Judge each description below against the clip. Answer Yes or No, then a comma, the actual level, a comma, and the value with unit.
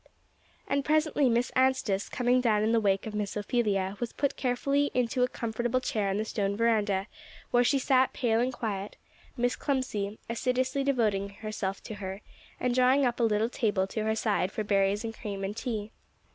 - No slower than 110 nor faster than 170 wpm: No, average, 190 wpm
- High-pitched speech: Yes, high, 225 Hz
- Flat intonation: No, average, 3.5 semitones